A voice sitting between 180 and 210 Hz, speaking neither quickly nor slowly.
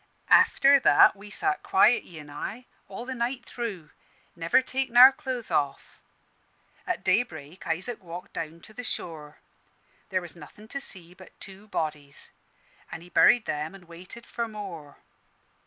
Yes: high, 190 Hz; average, 160 wpm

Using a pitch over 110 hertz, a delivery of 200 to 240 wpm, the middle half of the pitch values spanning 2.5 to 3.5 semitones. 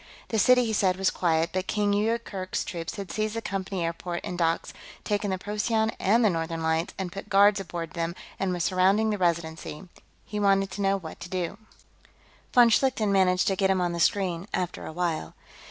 Yes: high, 190 Hz; fast, 205 wpm; average, 3.2 semitones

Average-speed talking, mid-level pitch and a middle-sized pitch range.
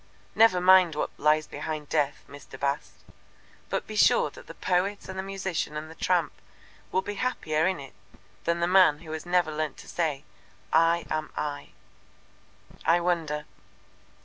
Yes: average, 165 wpm; medium, 165 Hz; average, 3.4 semitones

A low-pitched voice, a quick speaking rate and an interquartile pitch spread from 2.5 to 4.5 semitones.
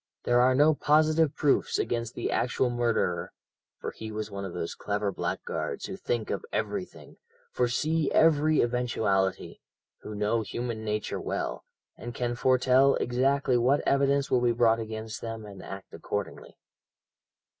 No: low, 120 Hz; average, 145 wpm; average, 3.7 semitones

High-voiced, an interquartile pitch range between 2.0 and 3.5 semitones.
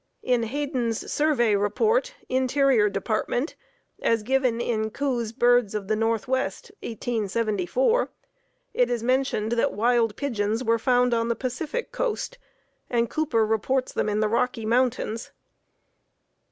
Yes: high, 235 Hz; average, 2.9 semitones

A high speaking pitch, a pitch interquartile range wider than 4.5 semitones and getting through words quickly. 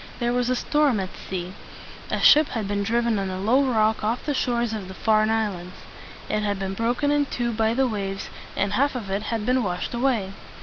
No: high, 220 Hz; average, 3.7 semitones; fast, 220 wpm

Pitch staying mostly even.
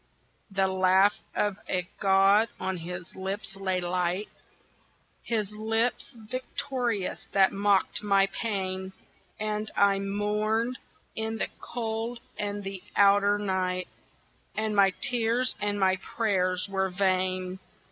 Yes: narrow, 2.3 semitones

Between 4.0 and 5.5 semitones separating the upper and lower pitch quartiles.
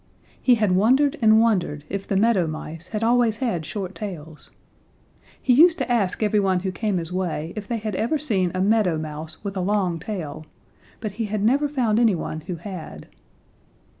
Yes: average, 4.3 semitones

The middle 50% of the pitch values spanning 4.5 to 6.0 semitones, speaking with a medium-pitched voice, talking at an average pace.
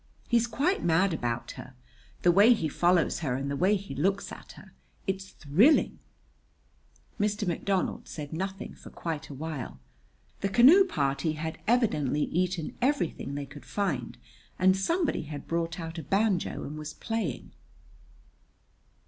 Yes: average, 5.2 semitones; medium, 175 Hz; average, 150 wpm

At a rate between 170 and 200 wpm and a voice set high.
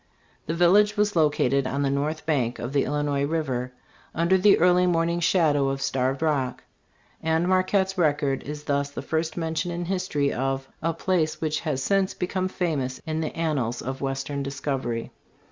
No: average, 175 wpm; medium, 155 Hz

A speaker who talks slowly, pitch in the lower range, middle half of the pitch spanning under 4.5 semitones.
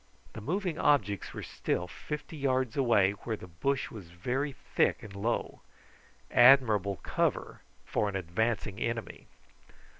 No: slow, 130 wpm; low, 115 Hz; average, 5.3 semitones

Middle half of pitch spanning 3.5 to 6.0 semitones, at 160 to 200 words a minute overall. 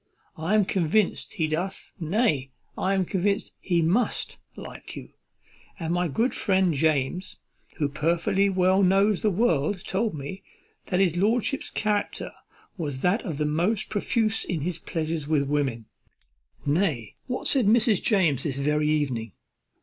No: average, 5.0 semitones; average, 150 wpm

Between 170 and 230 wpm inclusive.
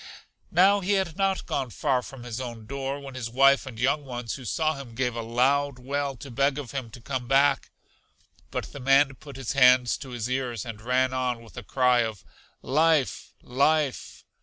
Yes: average, 200 wpm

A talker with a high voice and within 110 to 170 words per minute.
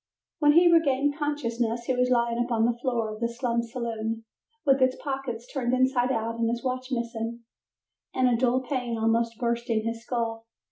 No: high, 240 Hz; average, 180 wpm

